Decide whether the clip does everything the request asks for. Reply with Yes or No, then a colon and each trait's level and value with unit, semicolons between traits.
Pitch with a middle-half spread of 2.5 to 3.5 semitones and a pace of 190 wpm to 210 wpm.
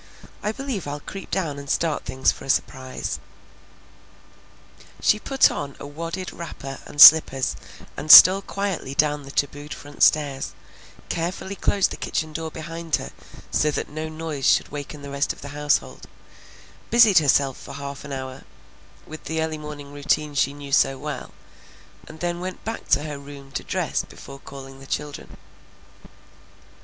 No: average, 2.8 semitones; average, 165 wpm